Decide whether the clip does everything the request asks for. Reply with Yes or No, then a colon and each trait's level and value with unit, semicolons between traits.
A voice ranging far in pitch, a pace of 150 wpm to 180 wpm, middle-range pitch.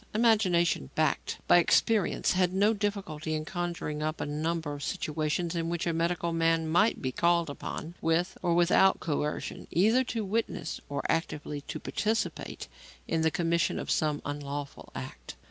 No: average, 3.2 semitones; average, 160 wpm; medium, 170 Hz